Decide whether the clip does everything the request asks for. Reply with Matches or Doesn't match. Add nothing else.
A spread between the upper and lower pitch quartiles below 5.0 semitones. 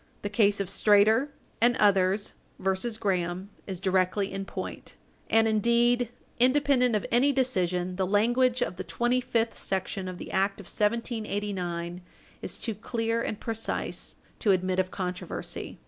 Matches